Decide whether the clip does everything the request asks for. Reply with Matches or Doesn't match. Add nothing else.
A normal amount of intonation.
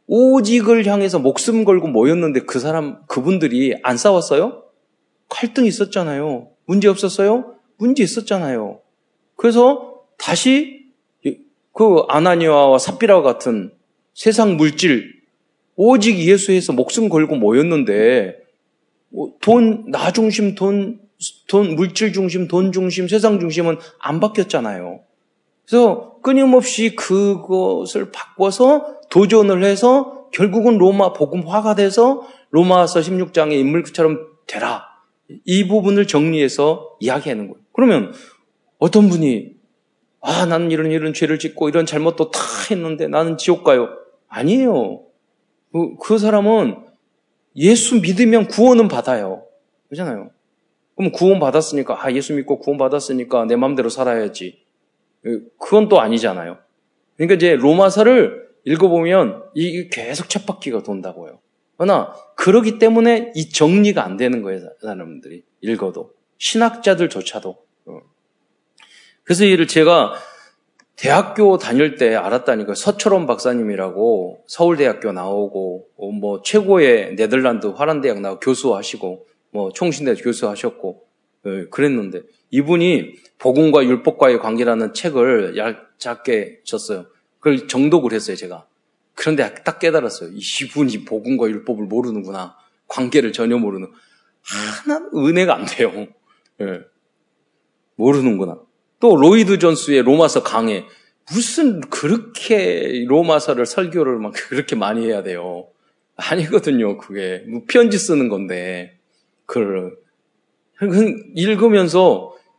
Doesn't match